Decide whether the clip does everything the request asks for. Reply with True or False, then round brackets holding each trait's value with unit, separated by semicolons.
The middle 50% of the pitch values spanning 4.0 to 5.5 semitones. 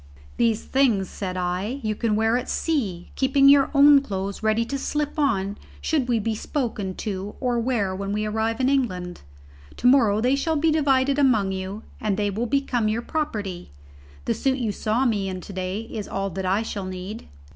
True (5.2 semitones)